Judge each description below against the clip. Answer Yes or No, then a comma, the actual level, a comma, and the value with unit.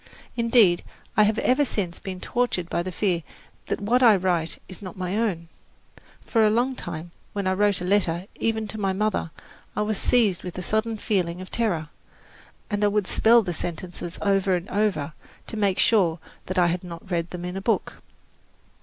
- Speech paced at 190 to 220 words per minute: Yes, average, 195 wpm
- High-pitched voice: Yes, high, 195 Hz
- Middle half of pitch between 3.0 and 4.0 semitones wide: Yes, average, 3.4 semitones